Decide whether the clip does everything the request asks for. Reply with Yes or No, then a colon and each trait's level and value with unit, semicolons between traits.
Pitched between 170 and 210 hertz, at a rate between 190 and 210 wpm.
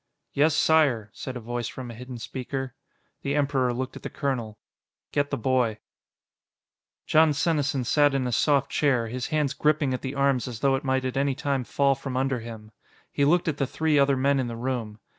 No: low, 135 Hz; fast, 205 wpm